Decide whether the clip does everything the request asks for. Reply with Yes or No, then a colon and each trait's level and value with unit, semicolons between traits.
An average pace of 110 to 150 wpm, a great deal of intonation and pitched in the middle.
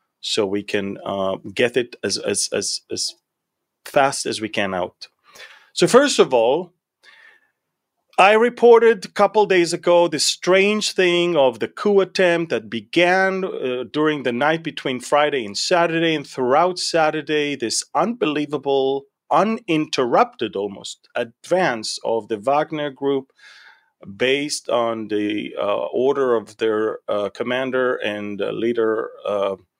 Yes: slow, 135 wpm; wide, 7.5 semitones; medium, 145 Hz